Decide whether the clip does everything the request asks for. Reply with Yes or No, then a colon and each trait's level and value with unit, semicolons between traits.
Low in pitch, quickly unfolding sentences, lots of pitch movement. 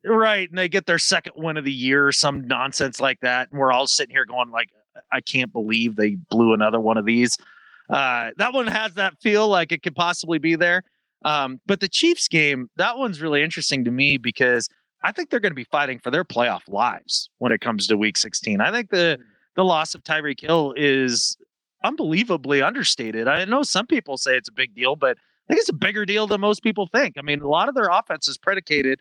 No: medium, 150 Hz; fast, 230 wpm; wide, 7.0 semitones